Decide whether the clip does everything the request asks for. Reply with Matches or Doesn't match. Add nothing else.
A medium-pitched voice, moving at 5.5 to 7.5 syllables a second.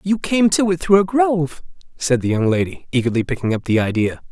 Matches